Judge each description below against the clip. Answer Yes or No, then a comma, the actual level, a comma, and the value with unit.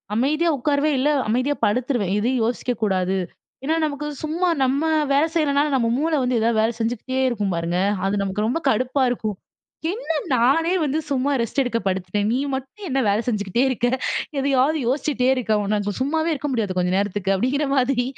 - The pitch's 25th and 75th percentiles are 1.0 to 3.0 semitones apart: No, average, 5.0 semitones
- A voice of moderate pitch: No, very high, 255 Hz